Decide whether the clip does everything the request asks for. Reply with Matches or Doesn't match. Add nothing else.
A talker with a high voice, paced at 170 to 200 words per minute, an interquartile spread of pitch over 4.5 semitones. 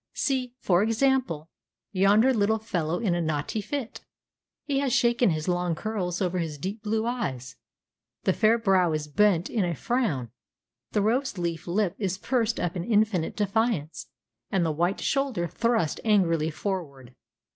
Doesn't match